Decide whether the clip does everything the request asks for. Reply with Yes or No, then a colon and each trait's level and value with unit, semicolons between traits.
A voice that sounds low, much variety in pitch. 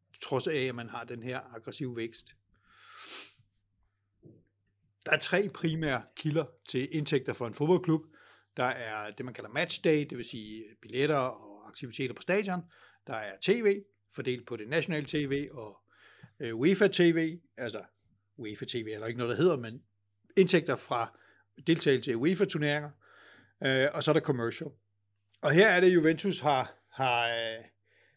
Yes: low, 130 Hz; wide, 5.9 semitones